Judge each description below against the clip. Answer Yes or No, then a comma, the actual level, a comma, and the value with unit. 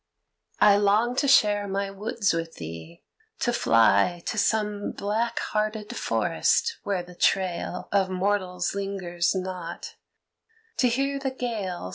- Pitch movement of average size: Yes, average, 3.3 semitones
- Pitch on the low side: No, high, 200 Hz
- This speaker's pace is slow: Yes, slow, 130 wpm